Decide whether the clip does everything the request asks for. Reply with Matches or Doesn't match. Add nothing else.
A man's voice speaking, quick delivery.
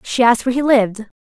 Doesn't match